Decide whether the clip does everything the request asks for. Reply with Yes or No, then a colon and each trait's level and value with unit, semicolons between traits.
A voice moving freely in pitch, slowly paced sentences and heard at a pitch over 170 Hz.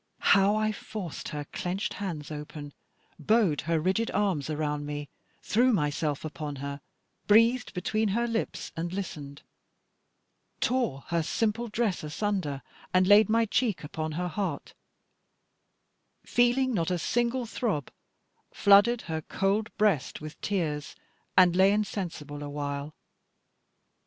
Yes: wide, 6.3 semitones; slow, 125 wpm; medium, 185 Hz